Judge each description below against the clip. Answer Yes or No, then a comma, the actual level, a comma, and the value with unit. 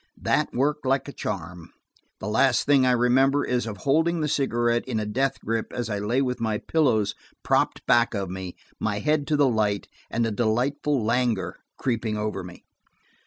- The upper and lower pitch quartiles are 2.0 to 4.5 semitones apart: Yes, average, 4.2 semitones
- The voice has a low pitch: Yes, low, 120 Hz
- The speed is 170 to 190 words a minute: Yes, average, 185 wpm